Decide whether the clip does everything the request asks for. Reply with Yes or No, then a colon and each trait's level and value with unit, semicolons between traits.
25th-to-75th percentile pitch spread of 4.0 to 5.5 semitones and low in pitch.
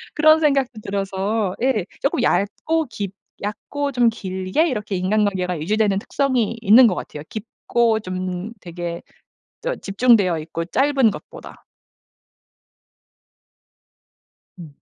No: average, 5.2 semitones; high, 210 Hz